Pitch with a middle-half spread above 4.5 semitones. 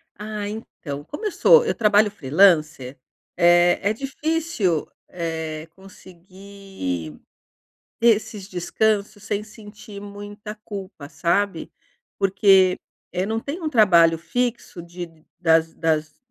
No: average, 4.1 semitones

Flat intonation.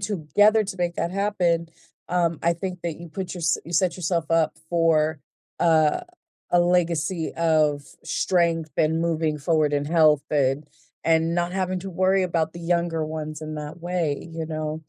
Yes: narrow, 2.1 semitones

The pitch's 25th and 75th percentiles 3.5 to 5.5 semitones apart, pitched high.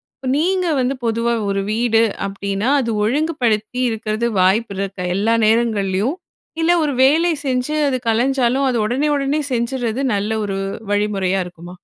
Yes: average, 4.6 semitones; high, 230 Hz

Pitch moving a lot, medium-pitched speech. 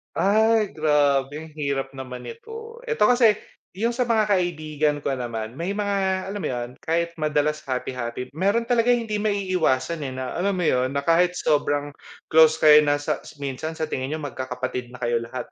Yes: wide, 7.0 semitones; medium, 155 Hz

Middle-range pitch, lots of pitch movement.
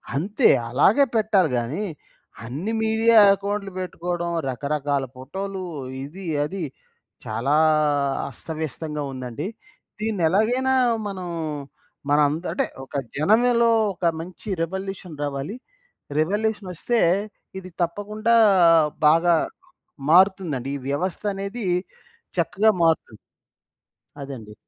Yes: medium, 180 Hz; wide, 5.7 semitones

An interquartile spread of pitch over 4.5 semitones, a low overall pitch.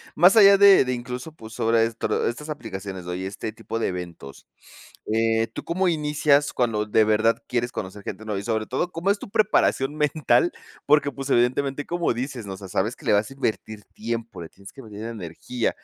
Yes: wide, 5.4 semitones; low, 115 Hz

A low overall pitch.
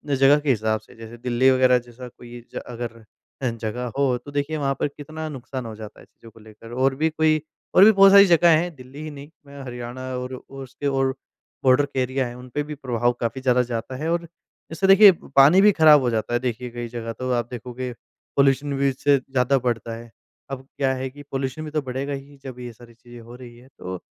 Yes: low, 130 Hz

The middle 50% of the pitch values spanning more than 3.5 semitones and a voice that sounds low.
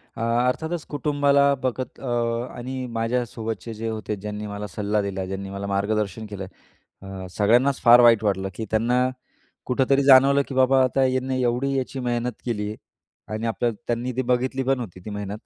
Yes: average, 3.9 semitones; low, 120 Hz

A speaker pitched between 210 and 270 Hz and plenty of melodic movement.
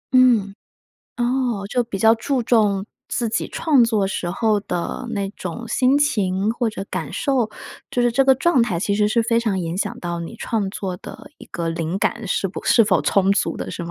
No: high, 215 Hz; average, 3.8 semitones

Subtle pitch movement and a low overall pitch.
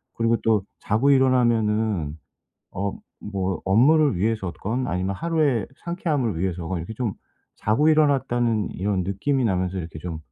No: wide, 5.5 semitones; low, 110 Hz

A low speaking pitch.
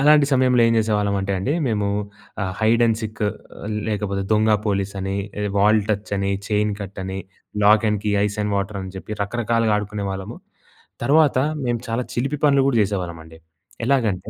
Yes: low, 105 Hz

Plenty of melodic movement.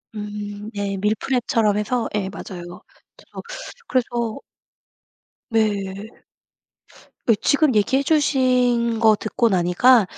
No: average, 3.3 semitones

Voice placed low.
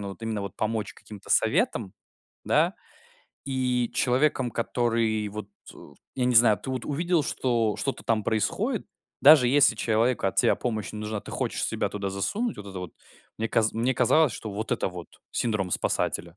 Yes: low, 115 Hz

